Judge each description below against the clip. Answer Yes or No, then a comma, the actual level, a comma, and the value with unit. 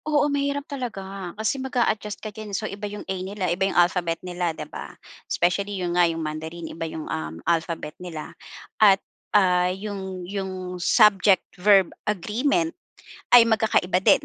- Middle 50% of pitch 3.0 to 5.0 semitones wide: Yes, average, 3.4 semitones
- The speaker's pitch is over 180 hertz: Yes, high, 190 Hz